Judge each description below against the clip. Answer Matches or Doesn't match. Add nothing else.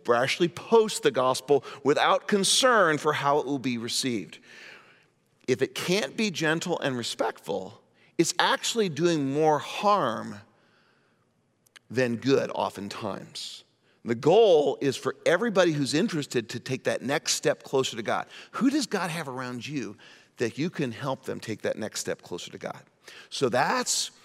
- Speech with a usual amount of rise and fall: Doesn't match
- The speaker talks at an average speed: Matches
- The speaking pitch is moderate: Matches